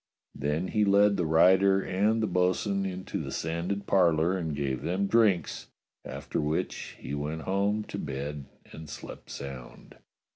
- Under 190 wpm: Yes, average, 150 wpm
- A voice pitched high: No, very low, 90 Hz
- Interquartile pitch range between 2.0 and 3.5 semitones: No, average, 4.5 semitones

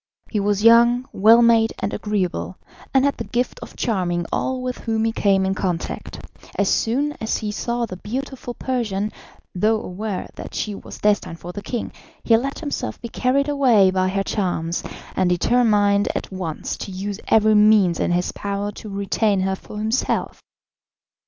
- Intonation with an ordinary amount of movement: Yes, average, 3.6 semitones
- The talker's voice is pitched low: No, high, 210 Hz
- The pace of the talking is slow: No, average, 175 wpm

